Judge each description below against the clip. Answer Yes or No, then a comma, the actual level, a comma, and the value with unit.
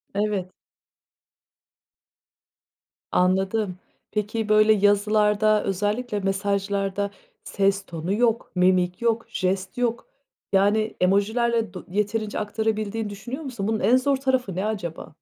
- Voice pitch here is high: Yes, high, 210 Hz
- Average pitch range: No, narrow, 2.2 semitones